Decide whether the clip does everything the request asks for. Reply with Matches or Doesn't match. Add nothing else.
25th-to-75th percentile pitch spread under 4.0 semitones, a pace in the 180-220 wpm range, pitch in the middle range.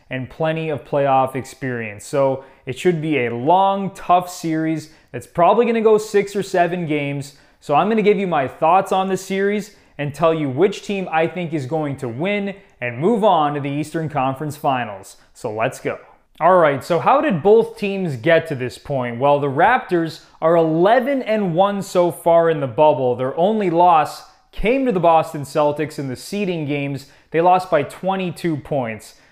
Doesn't match